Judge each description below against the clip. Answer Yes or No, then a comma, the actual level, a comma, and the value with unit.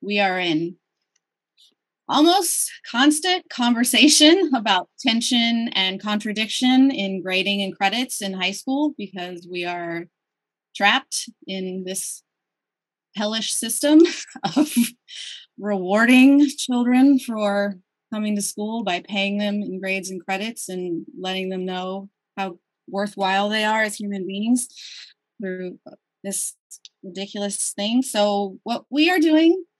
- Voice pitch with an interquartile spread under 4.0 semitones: No, average, 4.8 semitones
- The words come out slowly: Yes, slow, 120 wpm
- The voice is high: Yes, high, 205 Hz